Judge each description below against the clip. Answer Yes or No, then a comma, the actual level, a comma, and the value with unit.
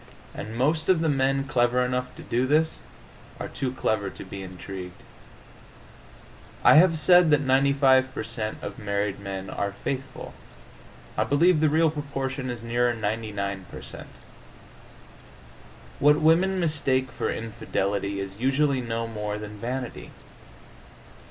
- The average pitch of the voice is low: Yes, low, 125 Hz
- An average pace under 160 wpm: Yes, average, 140 wpm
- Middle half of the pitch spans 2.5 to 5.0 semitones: No, wide, 5.5 semitones